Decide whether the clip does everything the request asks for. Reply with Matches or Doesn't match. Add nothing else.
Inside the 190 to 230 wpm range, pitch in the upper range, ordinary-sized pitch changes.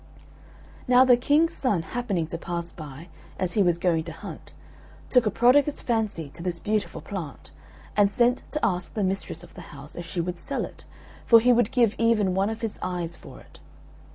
Doesn't match